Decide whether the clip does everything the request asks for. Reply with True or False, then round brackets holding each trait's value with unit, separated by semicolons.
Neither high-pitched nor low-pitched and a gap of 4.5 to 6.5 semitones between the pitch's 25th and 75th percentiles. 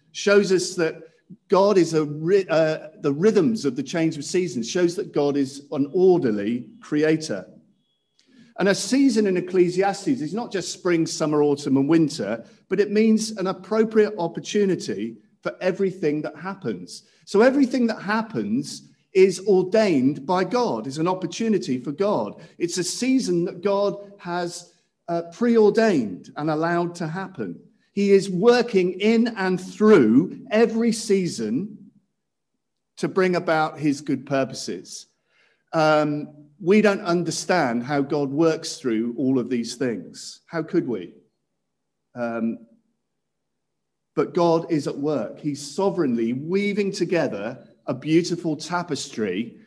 True (180 Hz; 5.1 semitones)